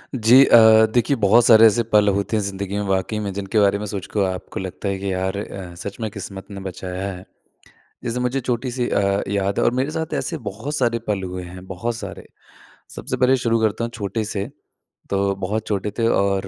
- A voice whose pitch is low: Yes, low, 100 Hz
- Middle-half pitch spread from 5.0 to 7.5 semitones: No, average, 3.1 semitones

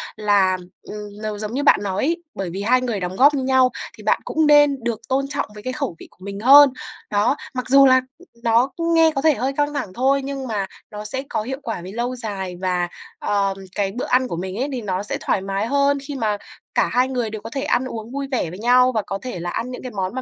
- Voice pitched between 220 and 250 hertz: Yes, high, 240 Hz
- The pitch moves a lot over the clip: No, average, 4.8 semitones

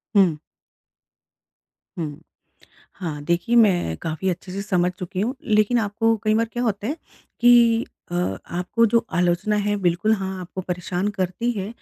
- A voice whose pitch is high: Yes, high, 195 Hz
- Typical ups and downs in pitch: Yes, average, 4.2 semitones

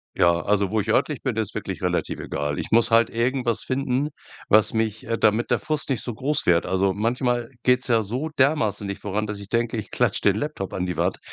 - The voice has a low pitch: Yes, low, 110 Hz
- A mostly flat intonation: No, average, 3.8 semitones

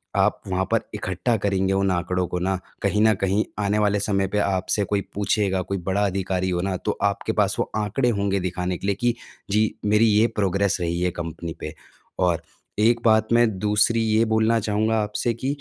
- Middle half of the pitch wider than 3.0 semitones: No, narrow, 2.5 semitones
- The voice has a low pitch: Yes, low, 100 Hz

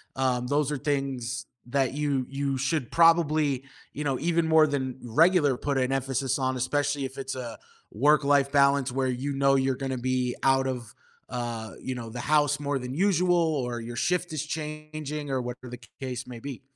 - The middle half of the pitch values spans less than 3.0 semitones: Yes, narrow, 2.5 semitones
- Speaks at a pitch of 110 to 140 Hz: Yes, low, 135 Hz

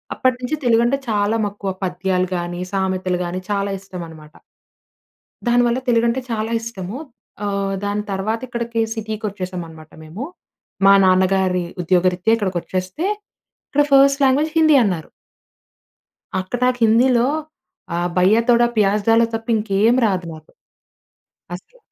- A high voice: Yes, high, 205 Hz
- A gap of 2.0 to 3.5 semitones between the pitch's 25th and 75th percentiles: No, average, 4.2 semitones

